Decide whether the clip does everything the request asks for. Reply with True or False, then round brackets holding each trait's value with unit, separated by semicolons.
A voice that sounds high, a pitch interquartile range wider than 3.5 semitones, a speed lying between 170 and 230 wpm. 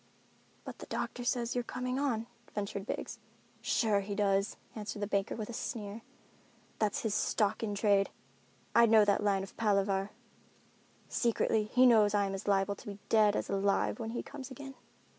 False (210 Hz; 2.6 semitones; 180 wpm)